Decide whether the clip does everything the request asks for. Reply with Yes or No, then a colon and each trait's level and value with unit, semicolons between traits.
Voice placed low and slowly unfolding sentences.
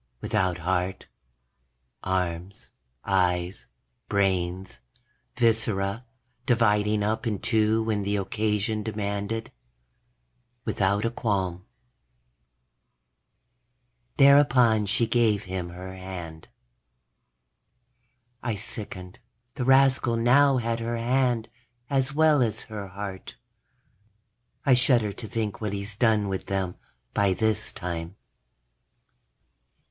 Yes: low, 105 Hz; slow, 95 wpm